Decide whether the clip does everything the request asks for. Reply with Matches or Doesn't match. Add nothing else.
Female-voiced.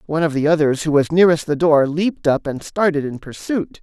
Doesn't match